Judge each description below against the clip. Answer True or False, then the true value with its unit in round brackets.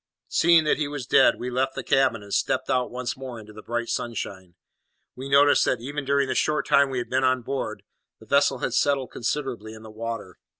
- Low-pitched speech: True (130 Hz)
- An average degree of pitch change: True (3.2 semitones)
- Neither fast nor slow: False (220 wpm)